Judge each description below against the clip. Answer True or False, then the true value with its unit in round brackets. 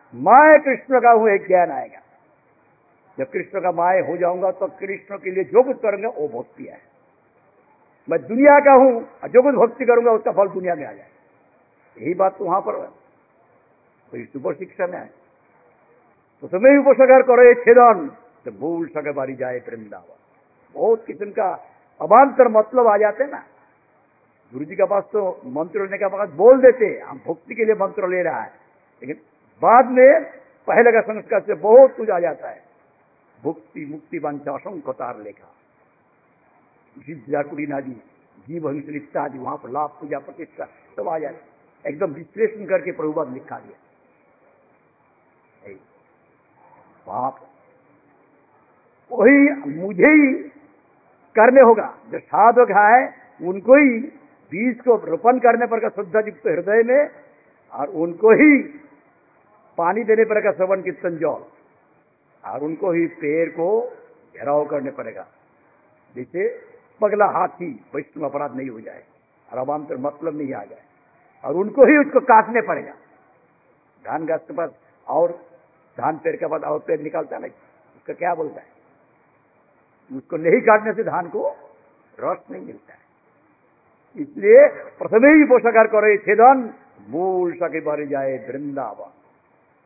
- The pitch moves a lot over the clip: True (7.7 semitones)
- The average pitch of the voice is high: True (215 Hz)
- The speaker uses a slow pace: False (145 wpm)